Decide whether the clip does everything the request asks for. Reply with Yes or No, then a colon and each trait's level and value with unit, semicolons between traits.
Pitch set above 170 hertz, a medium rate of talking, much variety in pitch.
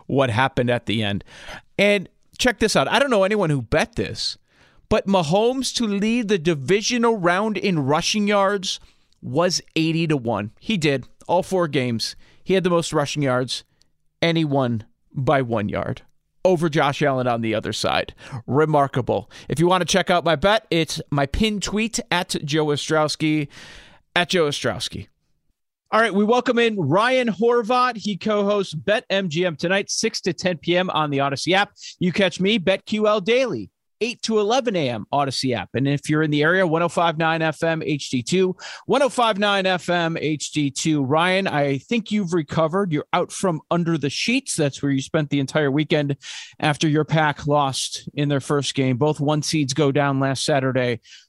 No: medium, 160 Hz; average, 175 wpm; wide, 5.7 semitones